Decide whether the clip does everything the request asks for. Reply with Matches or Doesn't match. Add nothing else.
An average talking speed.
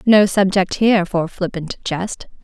Matches